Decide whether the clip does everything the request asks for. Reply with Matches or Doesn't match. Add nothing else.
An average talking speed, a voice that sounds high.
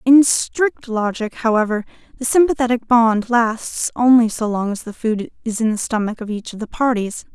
Matches